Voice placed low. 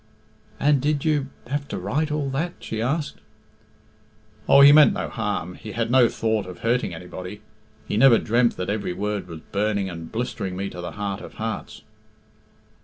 Yes: low, 110 Hz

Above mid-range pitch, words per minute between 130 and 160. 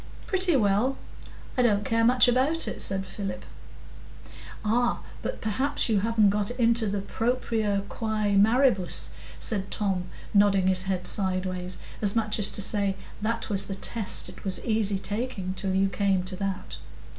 Yes: high, 205 Hz; average, 155 wpm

